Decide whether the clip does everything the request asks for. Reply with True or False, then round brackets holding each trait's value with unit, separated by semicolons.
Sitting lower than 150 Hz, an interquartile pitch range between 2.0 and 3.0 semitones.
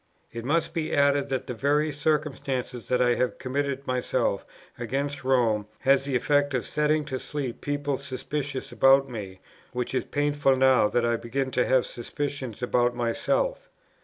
True (135 Hz; 2.6 semitones)